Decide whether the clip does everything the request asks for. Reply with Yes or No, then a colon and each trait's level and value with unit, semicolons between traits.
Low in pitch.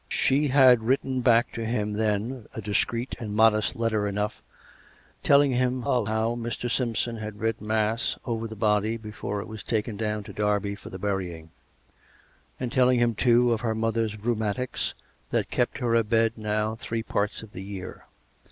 Yes: low, 110 Hz